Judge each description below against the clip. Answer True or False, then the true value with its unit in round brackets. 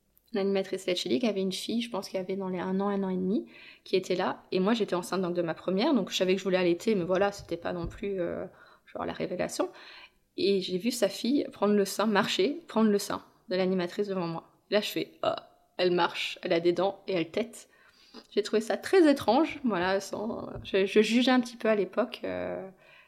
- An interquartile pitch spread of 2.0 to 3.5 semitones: True (2.7 semitones)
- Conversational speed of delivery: False (235 wpm)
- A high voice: True (195 Hz)